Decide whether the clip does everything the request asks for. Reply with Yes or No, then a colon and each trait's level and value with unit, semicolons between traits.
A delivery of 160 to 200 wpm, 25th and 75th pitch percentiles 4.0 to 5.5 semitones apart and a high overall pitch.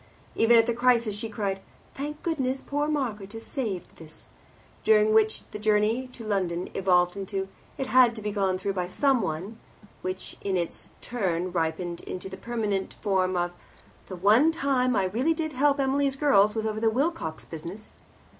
Yes: average, 175 wpm; average, 5.1 semitones; high, 215 Hz